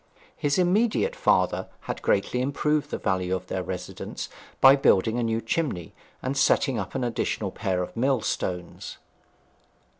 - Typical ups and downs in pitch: No, wide, 7.2 semitones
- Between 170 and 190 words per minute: No, average, 145 wpm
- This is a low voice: Yes, low, 120 Hz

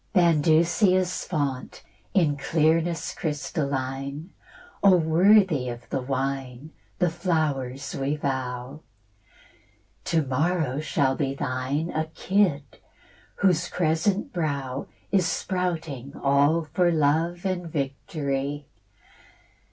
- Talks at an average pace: No, slow, 95 wpm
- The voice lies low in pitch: No, medium, 155 Hz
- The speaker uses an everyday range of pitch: Yes, average, 3.9 semitones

